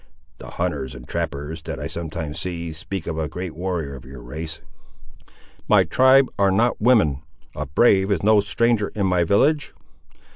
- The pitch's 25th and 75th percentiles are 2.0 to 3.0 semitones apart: No, average, 5.1 semitones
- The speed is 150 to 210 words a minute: Yes, average, 170 wpm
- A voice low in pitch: Yes, very low, 85 Hz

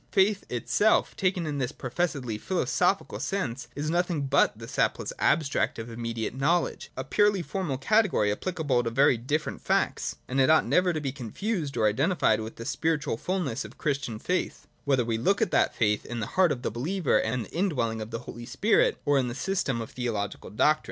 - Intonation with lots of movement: Yes, wide, 7.2 semitones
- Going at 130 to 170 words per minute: No, fast, 205 wpm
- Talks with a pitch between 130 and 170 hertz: Yes, medium, 140 Hz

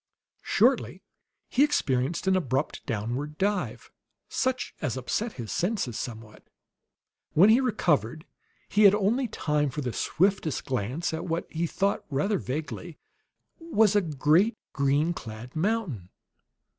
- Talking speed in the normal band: No, slow, 130 wpm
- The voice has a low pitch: No, medium, 160 Hz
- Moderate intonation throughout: No, wide, 7.4 semitones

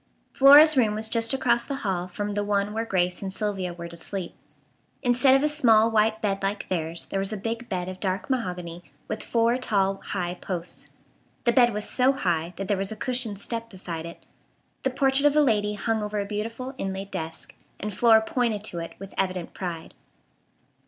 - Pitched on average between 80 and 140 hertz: No, high, 210 Hz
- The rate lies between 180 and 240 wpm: Yes, average, 200 wpm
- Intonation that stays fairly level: No, average, 4.0 semitones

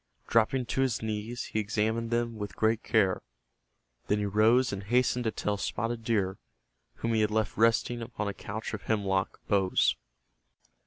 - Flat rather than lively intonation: Yes, narrow, 2.0 semitones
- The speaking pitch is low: Yes, low, 110 Hz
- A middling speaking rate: Yes, average, 165 wpm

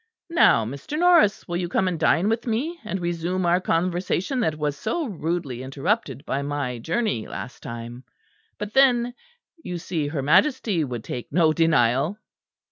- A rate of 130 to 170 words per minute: Yes, average, 160 wpm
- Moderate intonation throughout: No, wide, 7.2 semitones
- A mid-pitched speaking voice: Yes, medium, 170 Hz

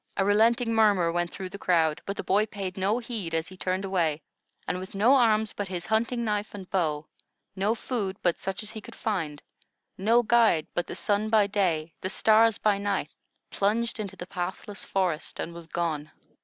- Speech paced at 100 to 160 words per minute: No, average, 195 wpm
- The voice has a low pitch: No, high, 195 Hz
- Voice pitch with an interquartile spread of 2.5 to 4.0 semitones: Yes, average, 3.6 semitones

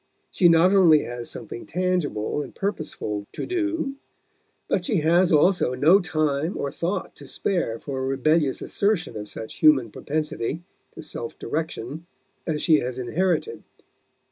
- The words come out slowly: No, average, 145 wpm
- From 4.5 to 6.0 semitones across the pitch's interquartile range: Yes, wide, 5.4 semitones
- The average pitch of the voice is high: No, medium, 155 Hz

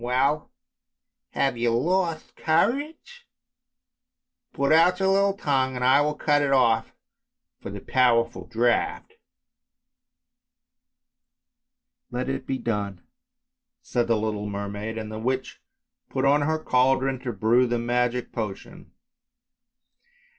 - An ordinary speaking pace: No, slow, 125 wpm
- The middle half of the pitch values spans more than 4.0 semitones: Yes, average, 4.9 semitones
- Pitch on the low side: Yes, low, 130 Hz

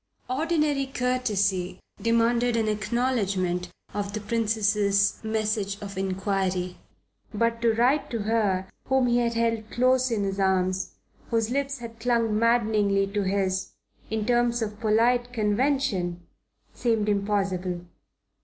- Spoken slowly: Yes, slow, 125 wpm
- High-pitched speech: Yes, high, 220 Hz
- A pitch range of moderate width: Yes, average, 3.2 semitones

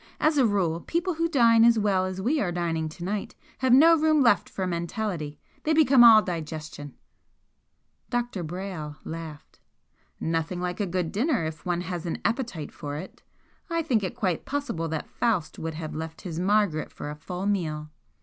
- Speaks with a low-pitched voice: No, medium, 185 Hz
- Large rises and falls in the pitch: Yes, wide, 6.3 semitones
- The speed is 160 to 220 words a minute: Yes, average, 180 wpm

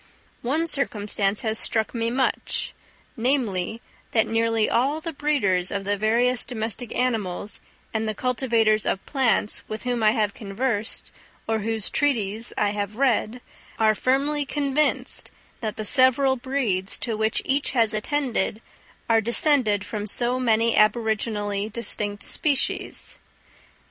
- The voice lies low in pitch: No, high, 225 Hz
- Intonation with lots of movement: No, average, 3.4 semitones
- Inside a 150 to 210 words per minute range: No, slow, 135 wpm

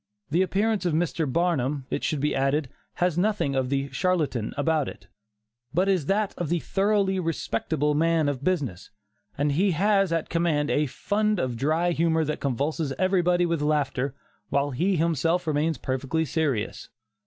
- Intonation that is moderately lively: Yes, average, 4.1 semitones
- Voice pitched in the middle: Yes, medium, 160 Hz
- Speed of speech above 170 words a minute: No, average, 165 wpm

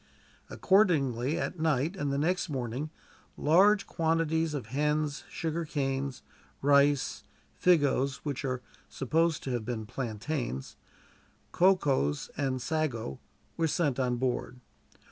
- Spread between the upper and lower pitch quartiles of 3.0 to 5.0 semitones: Yes, average, 4.1 semitones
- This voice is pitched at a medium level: Yes, medium, 145 Hz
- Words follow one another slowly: Yes, slow, 110 wpm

